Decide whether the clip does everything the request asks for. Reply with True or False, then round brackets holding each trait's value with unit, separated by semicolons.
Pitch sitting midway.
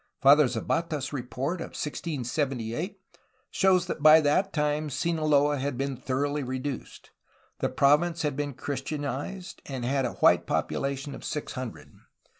True (145 Hz)